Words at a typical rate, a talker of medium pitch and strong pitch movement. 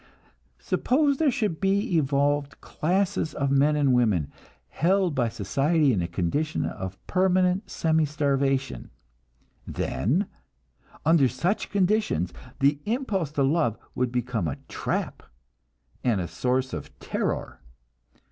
No: slow, 120 wpm; medium, 145 Hz; wide, 6.5 semitones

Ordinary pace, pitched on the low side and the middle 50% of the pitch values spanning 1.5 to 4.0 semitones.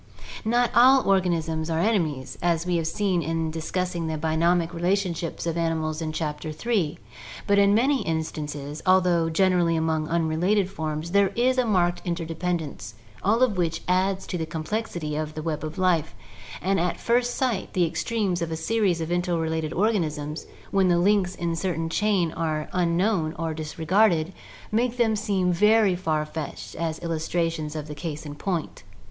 No: average, 170 wpm; medium, 170 Hz; average, 3.4 semitones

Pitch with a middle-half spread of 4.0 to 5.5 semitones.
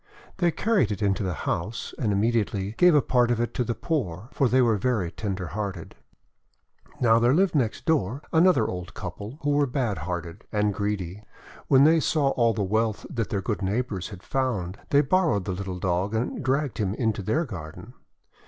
Yes: average, 5.1 semitones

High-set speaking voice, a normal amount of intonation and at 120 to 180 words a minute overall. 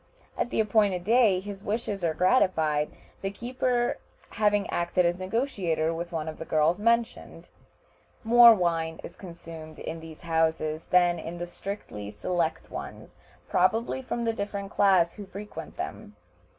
No: medium, 180 Hz; average, 4.4 semitones; average, 150 wpm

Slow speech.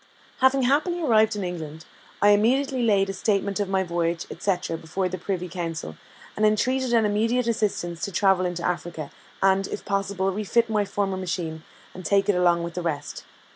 No: average, 180 wpm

